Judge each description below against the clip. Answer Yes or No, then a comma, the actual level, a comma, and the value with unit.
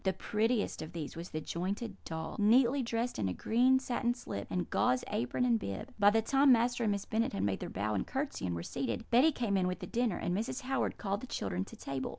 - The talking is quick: Yes, fast, 245 wpm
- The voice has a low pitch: No, high, 210 Hz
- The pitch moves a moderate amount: No, wide, 7.2 semitones